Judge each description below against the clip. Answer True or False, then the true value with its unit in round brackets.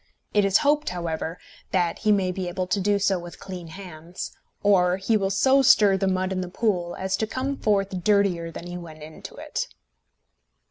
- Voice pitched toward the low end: False (190 Hz)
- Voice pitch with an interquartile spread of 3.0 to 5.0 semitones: False (2.5 semitones)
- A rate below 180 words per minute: False (195 wpm)